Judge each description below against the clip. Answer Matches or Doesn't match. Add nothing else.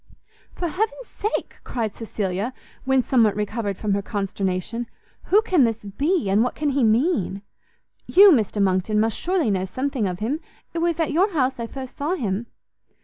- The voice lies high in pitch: Matches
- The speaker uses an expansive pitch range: Matches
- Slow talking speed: Doesn't match